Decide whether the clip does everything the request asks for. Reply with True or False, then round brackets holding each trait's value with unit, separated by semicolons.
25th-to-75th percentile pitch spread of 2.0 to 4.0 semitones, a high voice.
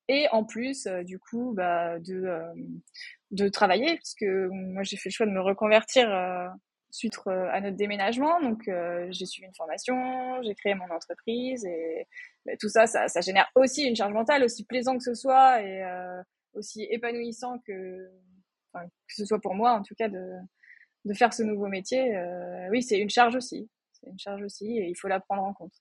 False (4.6 semitones; 205 Hz)